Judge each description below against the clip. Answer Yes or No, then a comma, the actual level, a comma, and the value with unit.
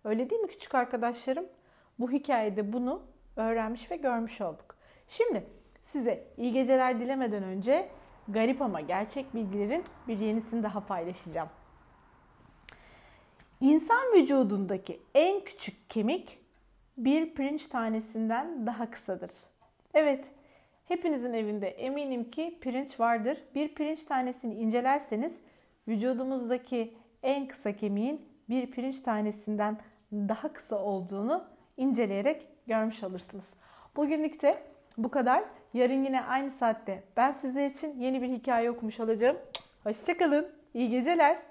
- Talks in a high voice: Yes, very high, 250 Hz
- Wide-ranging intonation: No, average, 4.4 semitones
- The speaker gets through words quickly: No, average, 115 wpm